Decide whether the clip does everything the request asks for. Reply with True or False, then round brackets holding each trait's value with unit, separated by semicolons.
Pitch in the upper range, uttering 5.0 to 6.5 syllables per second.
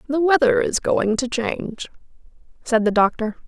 False (245 Hz; 4.8 syllables/s)